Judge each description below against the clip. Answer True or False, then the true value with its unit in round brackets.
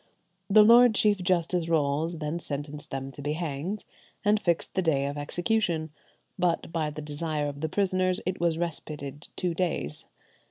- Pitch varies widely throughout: False (3.8 semitones)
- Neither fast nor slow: True (160 wpm)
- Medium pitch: True (165 Hz)